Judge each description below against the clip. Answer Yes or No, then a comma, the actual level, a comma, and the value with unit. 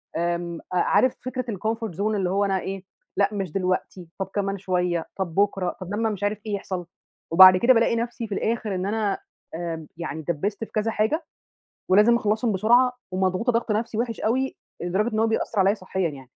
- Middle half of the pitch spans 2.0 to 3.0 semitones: No, average, 3.4 semitones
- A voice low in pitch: No, high, 200 Hz